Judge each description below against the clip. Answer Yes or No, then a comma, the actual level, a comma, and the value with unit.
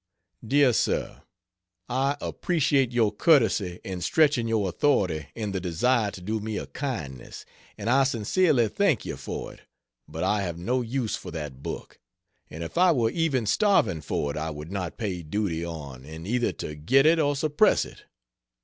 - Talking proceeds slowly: No, average, 175 wpm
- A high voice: No, low, 110 Hz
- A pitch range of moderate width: No, wide, 8.1 semitones